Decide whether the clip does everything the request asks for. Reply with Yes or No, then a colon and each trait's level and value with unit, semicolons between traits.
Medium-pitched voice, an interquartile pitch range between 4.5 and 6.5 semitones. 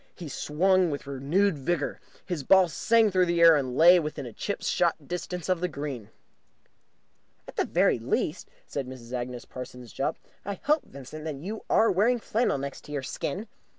Yes: medium, 155 Hz; average, 5.3 semitones